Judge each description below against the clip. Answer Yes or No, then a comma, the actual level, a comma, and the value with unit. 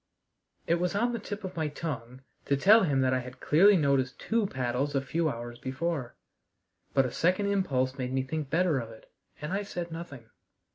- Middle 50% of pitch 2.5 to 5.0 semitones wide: No, wide, 5.6 semitones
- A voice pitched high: No, medium, 145 Hz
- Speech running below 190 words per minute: No, average, 200 wpm